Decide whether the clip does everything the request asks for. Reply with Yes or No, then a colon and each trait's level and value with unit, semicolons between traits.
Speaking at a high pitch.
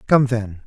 No: low, 115 Hz